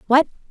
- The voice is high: Yes, very high, 275 Hz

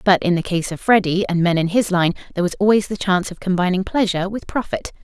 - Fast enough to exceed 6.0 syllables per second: Yes, 6.6 syllables/s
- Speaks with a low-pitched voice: No, medium, 185 Hz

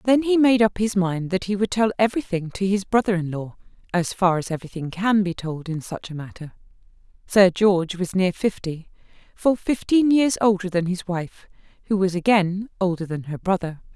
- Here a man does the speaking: No, female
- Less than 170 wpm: No, average, 200 wpm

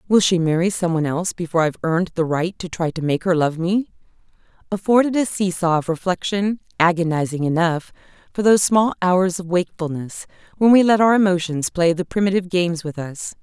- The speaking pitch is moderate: Yes, medium, 180 Hz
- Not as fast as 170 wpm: No, average, 190 wpm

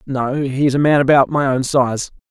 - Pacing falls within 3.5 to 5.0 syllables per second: Yes, 4.9 syllables/s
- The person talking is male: Yes, male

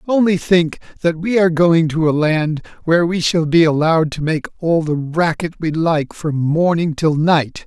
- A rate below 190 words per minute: No, average, 195 wpm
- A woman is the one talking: No, male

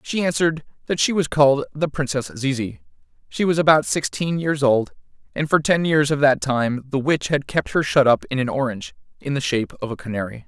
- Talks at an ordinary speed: No, fast, 220 wpm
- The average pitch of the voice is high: No, medium, 140 Hz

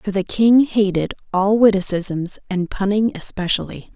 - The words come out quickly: No, slow, 135 wpm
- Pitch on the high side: Yes, high, 195 Hz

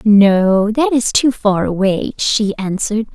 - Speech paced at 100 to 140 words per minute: Yes, slow, 135 wpm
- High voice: Yes, high, 215 Hz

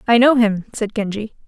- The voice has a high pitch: Yes, high, 220 Hz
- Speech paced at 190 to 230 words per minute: Yes, fast, 205 wpm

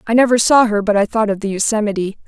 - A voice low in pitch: No, high, 215 Hz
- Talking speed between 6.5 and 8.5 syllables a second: Yes, 6.8 syllables/s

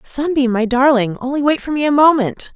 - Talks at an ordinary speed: Yes, average, 190 wpm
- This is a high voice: Yes, very high, 265 Hz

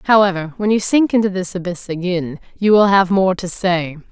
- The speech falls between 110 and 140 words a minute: No, fast, 205 wpm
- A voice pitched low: No, medium, 185 Hz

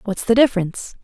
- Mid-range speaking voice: No, high, 210 Hz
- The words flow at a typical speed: Yes, average, 175 wpm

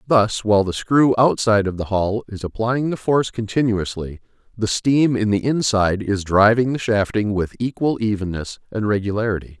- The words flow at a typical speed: Yes, average, 170 wpm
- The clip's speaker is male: Yes, male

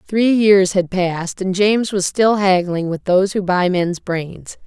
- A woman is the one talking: Yes, female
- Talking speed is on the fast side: No, average, 195 wpm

